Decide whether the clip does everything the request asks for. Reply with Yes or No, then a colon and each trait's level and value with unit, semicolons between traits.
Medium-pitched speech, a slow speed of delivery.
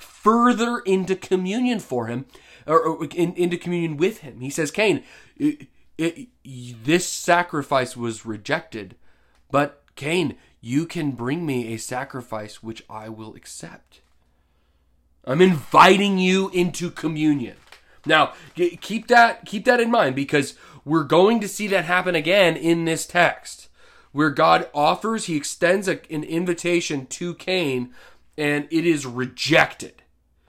Yes: medium, 160 Hz; slow, 130 wpm